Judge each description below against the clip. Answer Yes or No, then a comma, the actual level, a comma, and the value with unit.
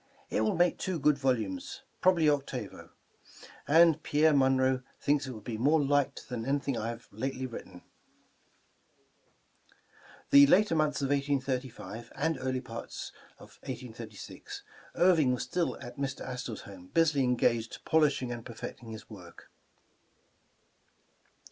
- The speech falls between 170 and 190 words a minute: No, average, 145 wpm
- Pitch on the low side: Yes, low, 130 Hz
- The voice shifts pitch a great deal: No, average, 3.9 semitones